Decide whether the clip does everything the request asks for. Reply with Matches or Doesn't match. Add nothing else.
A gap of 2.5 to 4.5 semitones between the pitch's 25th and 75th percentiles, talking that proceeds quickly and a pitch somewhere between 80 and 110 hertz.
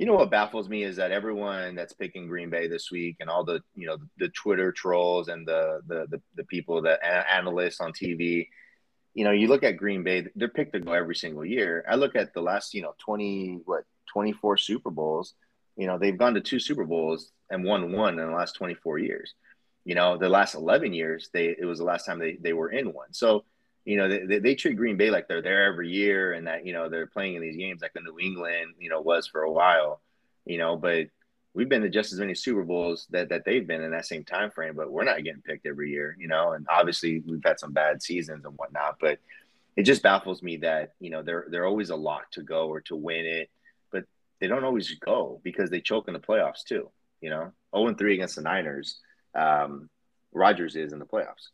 Matches